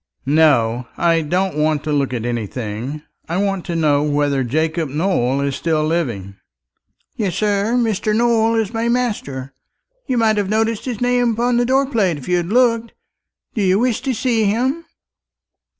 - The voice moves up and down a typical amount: No, wide, 7.8 semitones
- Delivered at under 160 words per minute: No, average, 170 wpm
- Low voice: No, medium, 185 Hz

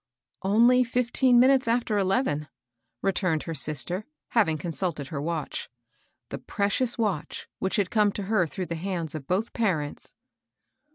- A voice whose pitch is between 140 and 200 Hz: Yes, high, 190 Hz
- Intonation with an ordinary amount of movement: No, wide, 6.0 semitones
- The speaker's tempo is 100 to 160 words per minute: Yes, average, 155 wpm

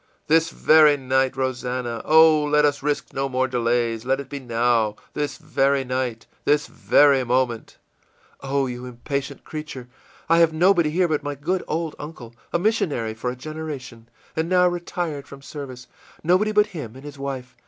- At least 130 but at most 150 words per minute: No, average, 175 wpm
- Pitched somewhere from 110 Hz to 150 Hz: Yes, medium, 140 Hz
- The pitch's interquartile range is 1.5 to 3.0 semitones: No, average, 3.7 semitones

